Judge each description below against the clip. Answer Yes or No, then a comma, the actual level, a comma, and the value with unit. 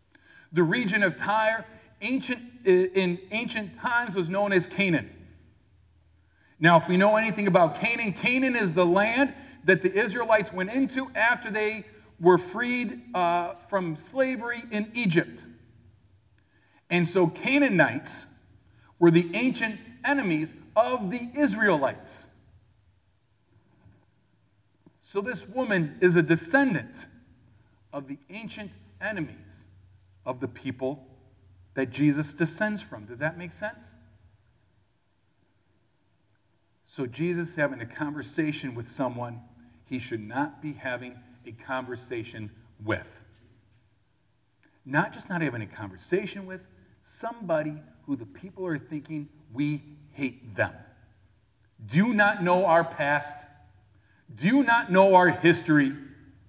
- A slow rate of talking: Yes, slow, 115 wpm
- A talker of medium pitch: Yes, medium, 150 Hz